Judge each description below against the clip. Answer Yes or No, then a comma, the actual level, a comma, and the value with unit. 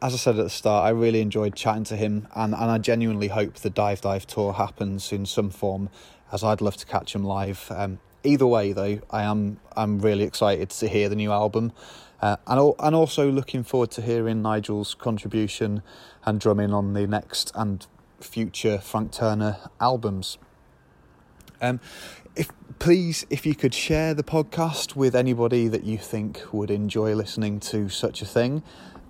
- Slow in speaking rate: No, average, 180 wpm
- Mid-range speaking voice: No, low, 110 Hz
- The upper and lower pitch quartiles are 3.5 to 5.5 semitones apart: No, narrow, 2.4 semitones